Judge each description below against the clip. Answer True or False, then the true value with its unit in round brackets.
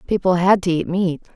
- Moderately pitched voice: True (180 Hz)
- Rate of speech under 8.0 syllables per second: True (5.5 syllables/s)